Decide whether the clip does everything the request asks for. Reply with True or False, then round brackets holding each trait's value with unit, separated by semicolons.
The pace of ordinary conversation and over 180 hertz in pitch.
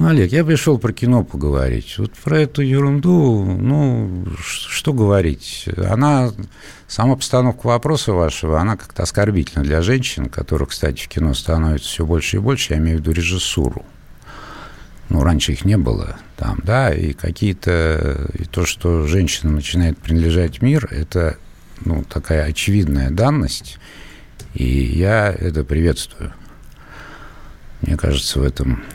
False (140 wpm; 90 Hz)